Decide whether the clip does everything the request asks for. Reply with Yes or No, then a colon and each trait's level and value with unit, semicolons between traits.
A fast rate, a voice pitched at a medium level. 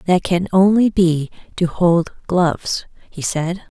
No: average, 145 wpm; medium, 175 Hz